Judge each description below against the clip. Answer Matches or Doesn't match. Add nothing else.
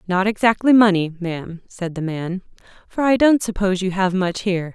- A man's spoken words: Doesn't match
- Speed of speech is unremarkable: Matches